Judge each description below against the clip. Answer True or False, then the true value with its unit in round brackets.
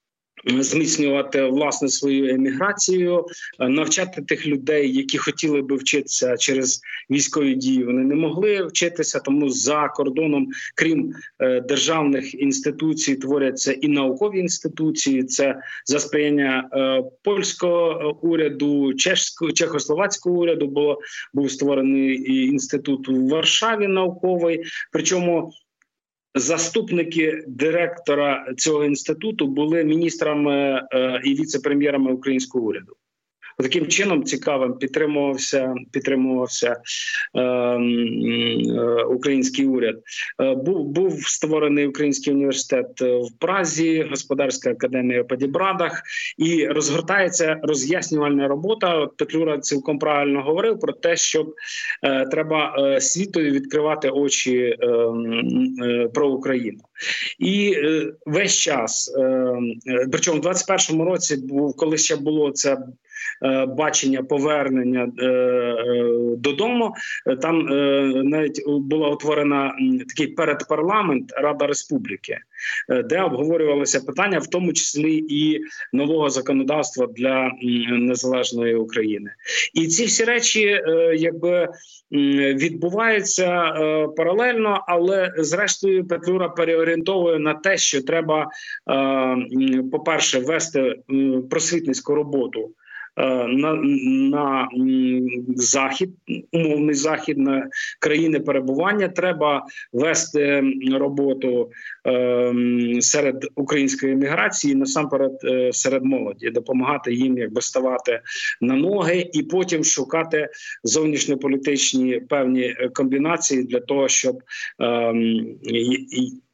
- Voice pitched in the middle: True (145 Hz)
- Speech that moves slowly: True (95 wpm)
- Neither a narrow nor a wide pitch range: True (3.9 semitones)